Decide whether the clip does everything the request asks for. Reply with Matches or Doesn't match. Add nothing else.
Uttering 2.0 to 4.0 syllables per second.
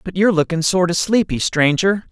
Doesn't match